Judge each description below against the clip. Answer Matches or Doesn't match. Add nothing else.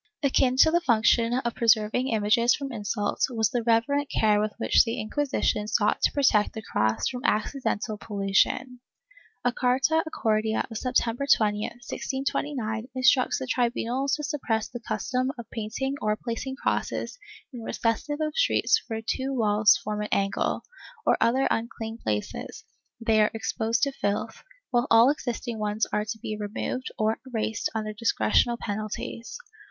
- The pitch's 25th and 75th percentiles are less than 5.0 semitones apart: Matches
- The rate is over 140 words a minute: Matches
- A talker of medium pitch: Doesn't match